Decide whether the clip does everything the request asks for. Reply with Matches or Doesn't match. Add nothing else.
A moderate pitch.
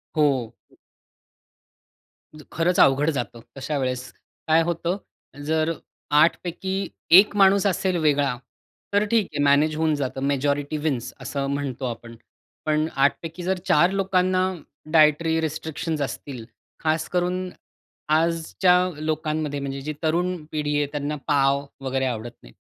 Matches